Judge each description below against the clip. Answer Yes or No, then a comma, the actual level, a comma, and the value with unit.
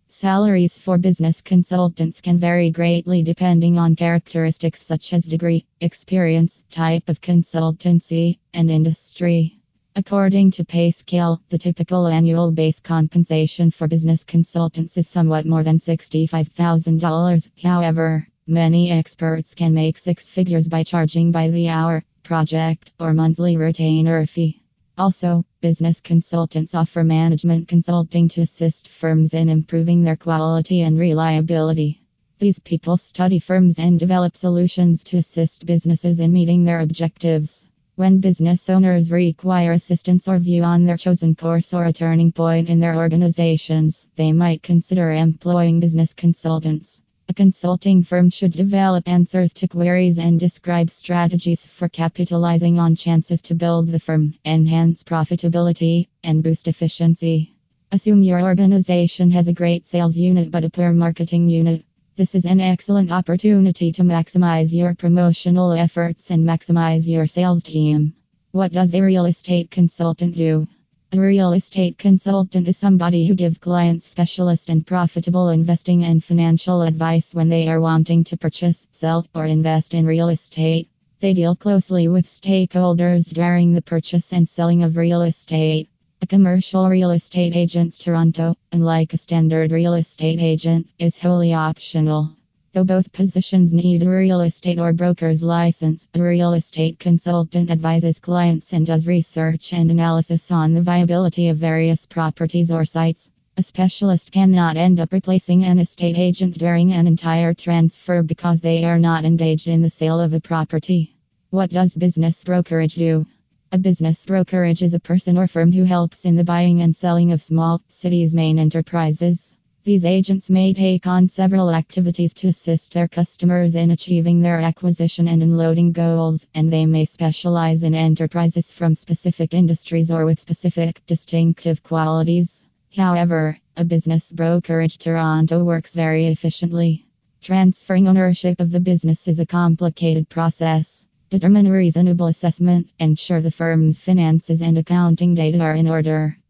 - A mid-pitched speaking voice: Yes, medium, 170 Hz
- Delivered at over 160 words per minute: No, average, 150 wpm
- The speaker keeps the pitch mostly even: Yes, narrow, 1.4 semitones